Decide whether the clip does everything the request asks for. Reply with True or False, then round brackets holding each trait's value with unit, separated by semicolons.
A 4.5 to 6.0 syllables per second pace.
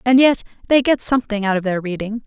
False (6.4 syllables/s)